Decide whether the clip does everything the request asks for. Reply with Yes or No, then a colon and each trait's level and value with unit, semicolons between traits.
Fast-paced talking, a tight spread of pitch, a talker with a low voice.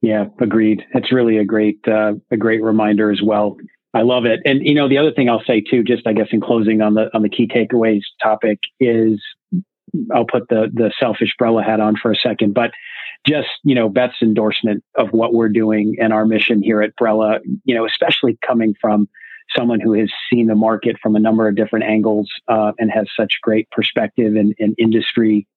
Yes: fast, 210 wpm; narrow, 1.4 semitones; low, 110 Hz